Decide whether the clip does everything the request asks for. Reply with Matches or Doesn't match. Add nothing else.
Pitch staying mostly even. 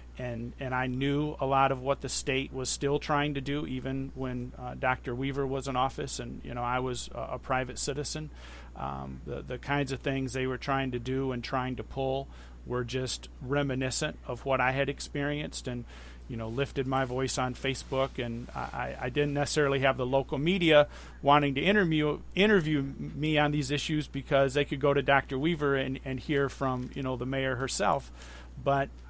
Matches